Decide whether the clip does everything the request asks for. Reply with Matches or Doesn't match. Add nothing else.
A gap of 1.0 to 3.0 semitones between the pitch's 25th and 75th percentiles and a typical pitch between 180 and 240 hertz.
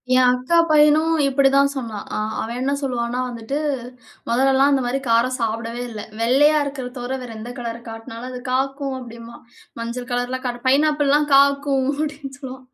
Doesn't match